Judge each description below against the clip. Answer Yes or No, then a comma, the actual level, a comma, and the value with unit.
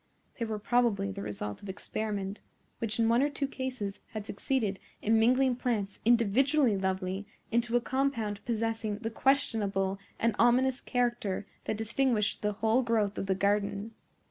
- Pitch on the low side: No, high, 220 Hz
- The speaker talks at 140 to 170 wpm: Yes, average, 155 wpm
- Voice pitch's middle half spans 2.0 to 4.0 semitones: Yes, average, 3.2 semitones